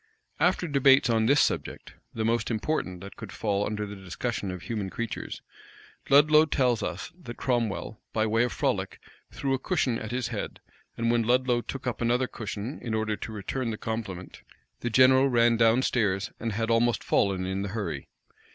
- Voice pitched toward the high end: No, low, 115 Hz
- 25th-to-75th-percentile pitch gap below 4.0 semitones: Yes, average, 3.2 semitones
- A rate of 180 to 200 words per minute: Yes, average, 185 wpm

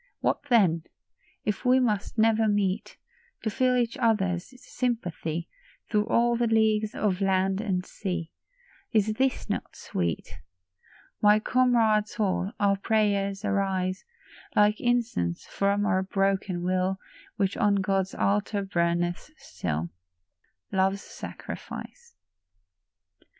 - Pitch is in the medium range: No, high, 200 Hz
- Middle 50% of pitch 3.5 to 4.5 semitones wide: No, average, 2.8 semitones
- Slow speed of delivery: Yes, slow, 115 wpm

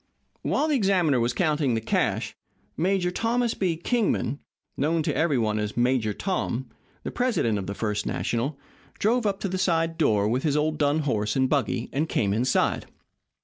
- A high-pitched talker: No, medium, 150 Hz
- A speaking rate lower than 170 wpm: No, average, 180 wpm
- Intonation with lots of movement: Yes, wide, 7.6 semitones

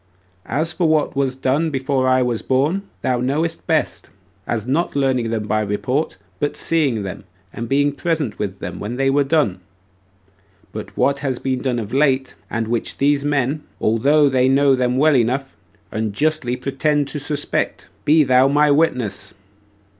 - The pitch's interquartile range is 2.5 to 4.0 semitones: Yes, average, 3.1 semitones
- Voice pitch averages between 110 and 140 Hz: Yes, low, 135 Hz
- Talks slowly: No, average, 170 wpm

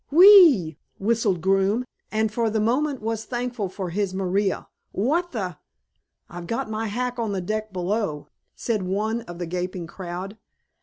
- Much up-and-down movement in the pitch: No, average, 3.9 semitones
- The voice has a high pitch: Yes, high, 210 Hz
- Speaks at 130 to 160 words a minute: No, average, 170 wpm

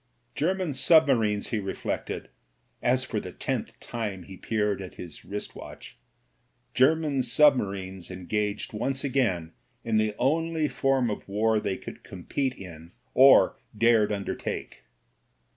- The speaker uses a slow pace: Yes, slow, 125 wpm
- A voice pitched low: Yes, low, 110 Hz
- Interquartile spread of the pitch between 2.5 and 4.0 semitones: No, wide, 5.5 semitones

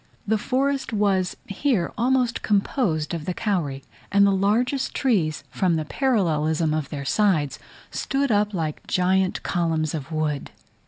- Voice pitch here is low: No, high, 190 Hz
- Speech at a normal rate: Yes, average, 145 wpm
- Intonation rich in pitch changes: Yes, wide, 5.8 semitones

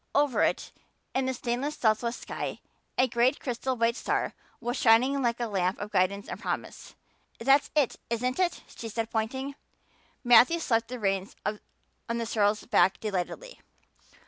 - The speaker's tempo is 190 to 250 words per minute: No, average, 155 wpm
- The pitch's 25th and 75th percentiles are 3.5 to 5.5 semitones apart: No, average, 3.1 semitones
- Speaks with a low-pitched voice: No, high, 235 Hz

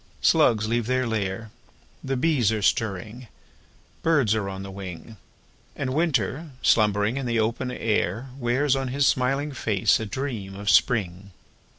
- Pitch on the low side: Yes, low, 115 Hz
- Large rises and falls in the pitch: No, average, 4.4 semitones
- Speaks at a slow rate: No, average, 145 wpm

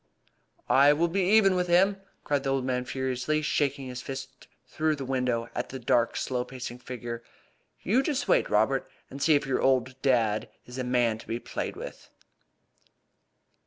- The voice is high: No, low, 130 Hz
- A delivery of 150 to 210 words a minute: Yes, average, 175 wpm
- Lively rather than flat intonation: No, average, 3.4 semitones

